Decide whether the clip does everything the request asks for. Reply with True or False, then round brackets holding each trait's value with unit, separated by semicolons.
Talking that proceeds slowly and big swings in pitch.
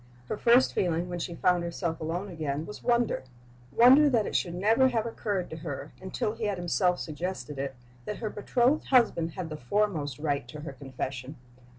False (190 wpm; 5.8 semitones)